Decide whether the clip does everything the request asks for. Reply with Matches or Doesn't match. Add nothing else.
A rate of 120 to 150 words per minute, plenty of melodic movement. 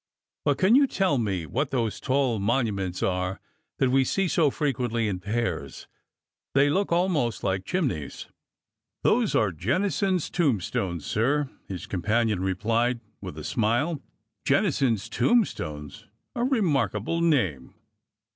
Matches